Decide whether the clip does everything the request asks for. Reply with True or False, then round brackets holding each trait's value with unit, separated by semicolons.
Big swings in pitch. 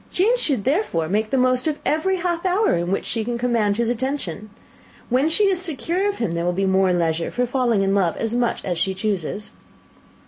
True (8.1 semitones)